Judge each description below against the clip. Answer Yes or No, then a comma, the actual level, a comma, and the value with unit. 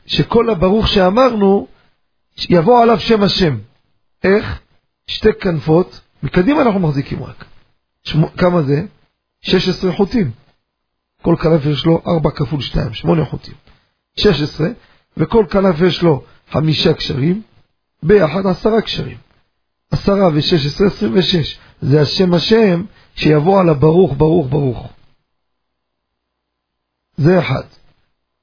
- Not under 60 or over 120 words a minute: Yes, average, 110 wpm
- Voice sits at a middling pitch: Yes, medium, 165 Hz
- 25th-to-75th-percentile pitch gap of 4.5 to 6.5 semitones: Yes, wide, 5.4 semitones